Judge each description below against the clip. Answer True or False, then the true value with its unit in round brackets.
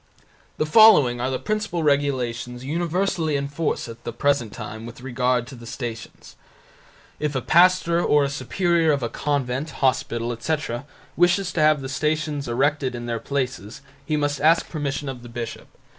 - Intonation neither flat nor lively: True (4.1 semitones)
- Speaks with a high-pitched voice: False (140 Hz)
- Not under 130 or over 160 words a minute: False (170 wpm)